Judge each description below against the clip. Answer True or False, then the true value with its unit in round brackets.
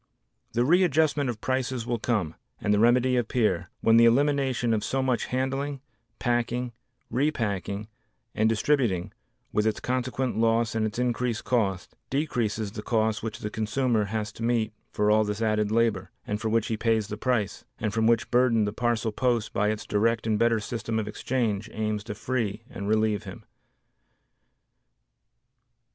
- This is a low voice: True (115 Hz)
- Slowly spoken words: False (165 wpm)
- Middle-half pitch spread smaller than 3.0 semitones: True (2.6 semitones)